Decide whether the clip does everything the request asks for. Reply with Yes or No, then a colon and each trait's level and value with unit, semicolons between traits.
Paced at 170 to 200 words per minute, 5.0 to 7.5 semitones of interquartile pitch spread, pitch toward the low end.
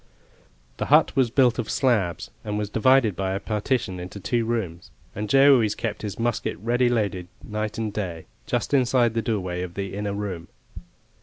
No: average, 180 wpm; average, 3.5 semitones; low, 105 Hz